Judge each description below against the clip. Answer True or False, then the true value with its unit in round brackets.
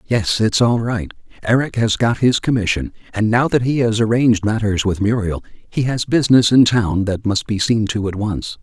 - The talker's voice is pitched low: True (110 Hz)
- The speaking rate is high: True (210 wpm)